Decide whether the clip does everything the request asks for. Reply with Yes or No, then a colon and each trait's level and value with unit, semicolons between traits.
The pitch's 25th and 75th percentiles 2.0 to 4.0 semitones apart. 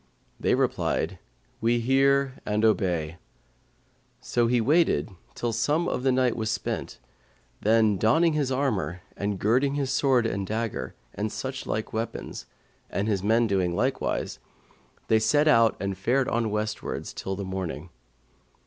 No: average, 4.5 semitones